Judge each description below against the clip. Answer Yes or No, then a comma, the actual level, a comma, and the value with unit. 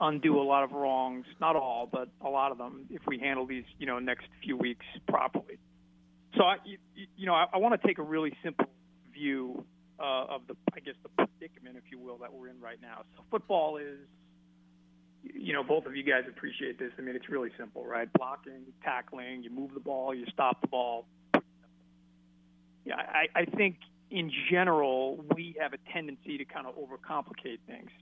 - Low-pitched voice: Yes, low, 130 Hz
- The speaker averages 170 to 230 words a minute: Yes, average, 200 wpm